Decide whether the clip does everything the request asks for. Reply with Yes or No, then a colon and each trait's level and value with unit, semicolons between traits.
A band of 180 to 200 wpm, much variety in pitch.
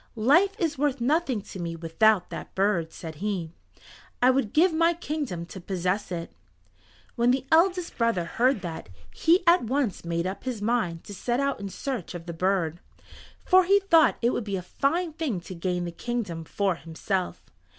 Yes: average, 185 wpm; wide, 8.0 semitones